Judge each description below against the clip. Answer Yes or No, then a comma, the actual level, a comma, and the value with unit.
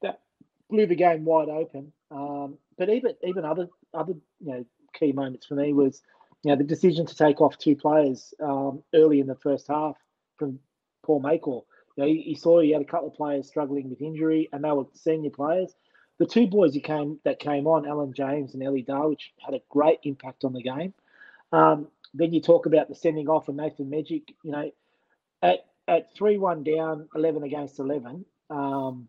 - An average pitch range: No, narrow, 2.3 semitones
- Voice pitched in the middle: Yes, medium, 150 Hz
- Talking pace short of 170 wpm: No, average, 200 wpm